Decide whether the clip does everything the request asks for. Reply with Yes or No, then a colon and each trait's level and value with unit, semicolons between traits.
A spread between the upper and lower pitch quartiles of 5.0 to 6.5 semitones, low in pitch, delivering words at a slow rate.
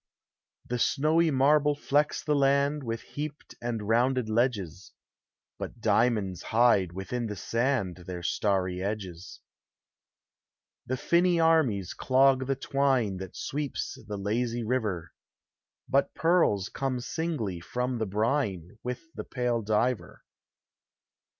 Yes: wide, 5.4 semitones; low, 120 Hz; slow, 120 wpm